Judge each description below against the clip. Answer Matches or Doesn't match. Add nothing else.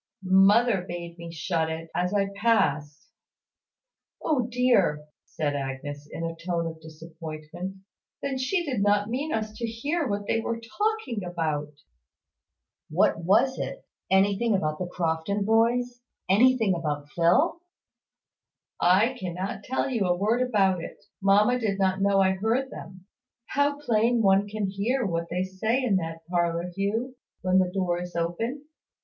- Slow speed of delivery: Doesn't match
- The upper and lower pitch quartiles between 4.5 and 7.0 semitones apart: Matches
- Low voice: Doesn't match